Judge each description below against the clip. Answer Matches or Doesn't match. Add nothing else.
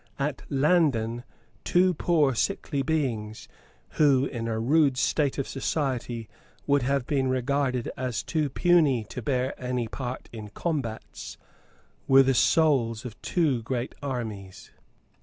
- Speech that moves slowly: Matches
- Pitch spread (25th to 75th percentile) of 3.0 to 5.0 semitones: Matches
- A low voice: Matches